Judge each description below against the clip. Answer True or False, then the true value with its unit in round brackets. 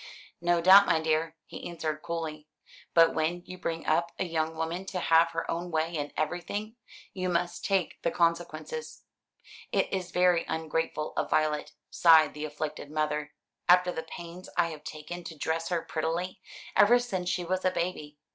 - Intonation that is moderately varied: False (2.1 semitones)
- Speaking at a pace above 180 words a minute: False (175 wpm)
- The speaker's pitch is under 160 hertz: False (165 Hz)